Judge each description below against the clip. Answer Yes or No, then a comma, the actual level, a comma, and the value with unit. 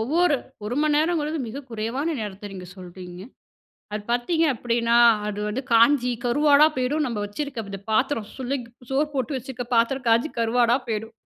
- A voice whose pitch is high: Yes, high, 245 Hz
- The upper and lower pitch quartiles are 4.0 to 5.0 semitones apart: Yes, average, 4.3 semitones